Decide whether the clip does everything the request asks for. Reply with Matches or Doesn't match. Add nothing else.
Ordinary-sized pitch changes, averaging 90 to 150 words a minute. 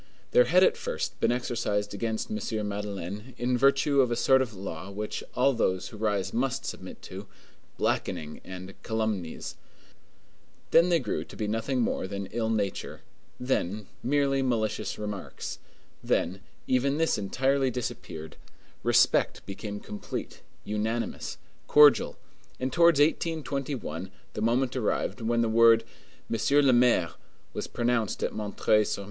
Matches